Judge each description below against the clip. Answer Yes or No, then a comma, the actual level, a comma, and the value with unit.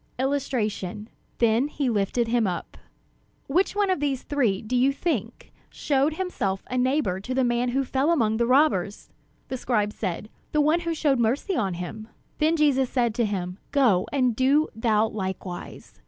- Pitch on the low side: No, very high, 250 Hz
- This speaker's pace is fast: No, average, 175 wpm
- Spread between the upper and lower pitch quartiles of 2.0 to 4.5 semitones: No, average, 5.0 semitones